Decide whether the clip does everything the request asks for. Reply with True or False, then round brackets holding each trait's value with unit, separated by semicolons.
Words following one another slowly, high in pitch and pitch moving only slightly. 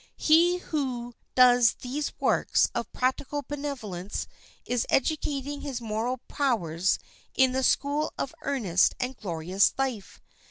False (120 wpm; 255 Hz; 4.3 semitones)